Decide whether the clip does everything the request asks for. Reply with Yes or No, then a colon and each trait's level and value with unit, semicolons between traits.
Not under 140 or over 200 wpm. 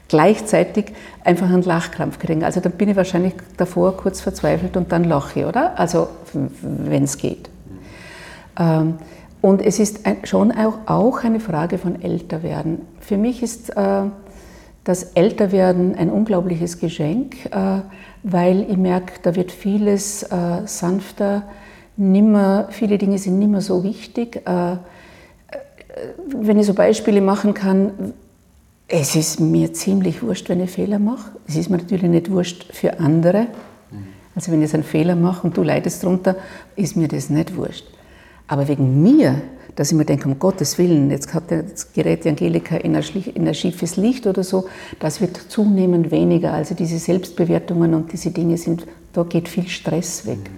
Yes: average, 155 wpm